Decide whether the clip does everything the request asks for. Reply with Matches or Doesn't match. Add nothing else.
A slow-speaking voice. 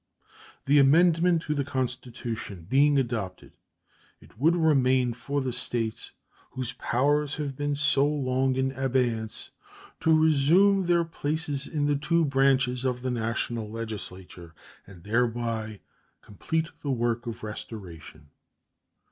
Matches